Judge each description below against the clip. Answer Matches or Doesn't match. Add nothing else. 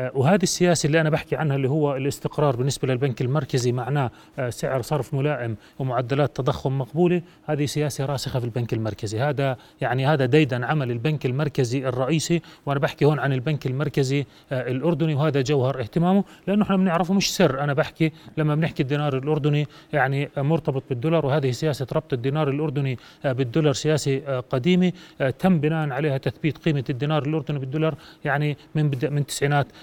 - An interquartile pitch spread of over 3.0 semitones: Doesn't match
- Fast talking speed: Matches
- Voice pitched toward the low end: Doesn't match